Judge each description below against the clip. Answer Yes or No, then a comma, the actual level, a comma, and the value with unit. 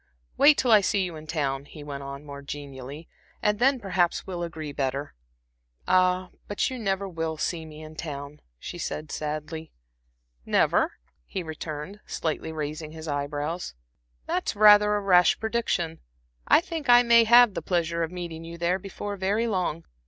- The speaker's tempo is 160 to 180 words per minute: Yes, average, 170 wpm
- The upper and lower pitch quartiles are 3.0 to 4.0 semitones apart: No, average, 4.8 semitones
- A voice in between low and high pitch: Yes, medium, 170 Hz